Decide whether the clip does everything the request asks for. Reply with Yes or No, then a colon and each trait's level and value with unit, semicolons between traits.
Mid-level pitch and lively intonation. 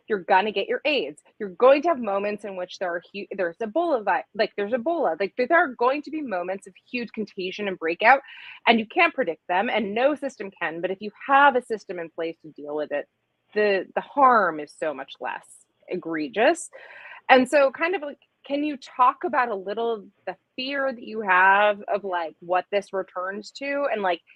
No: high, 210 Hz; wide, 6.1 semitones